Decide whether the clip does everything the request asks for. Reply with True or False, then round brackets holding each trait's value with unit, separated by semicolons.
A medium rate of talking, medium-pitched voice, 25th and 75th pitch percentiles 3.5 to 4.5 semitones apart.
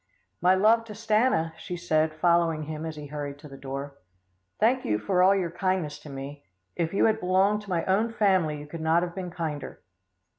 False (210 wpm; 170 Hz; 4.2 semitones)